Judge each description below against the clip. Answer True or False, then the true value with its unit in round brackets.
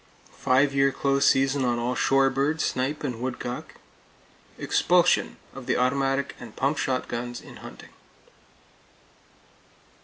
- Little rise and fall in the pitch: True (1.7 semitones)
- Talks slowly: True (120 wpm)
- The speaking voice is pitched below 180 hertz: True (135 Hz)